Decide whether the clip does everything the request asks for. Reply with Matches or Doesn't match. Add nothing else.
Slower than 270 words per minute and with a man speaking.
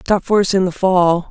Doesn't match